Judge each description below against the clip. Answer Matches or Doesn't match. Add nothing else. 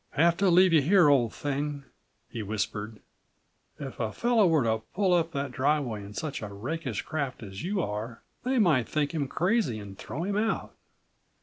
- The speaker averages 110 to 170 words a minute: Doesn't match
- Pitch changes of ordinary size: Doesn't match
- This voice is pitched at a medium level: Matches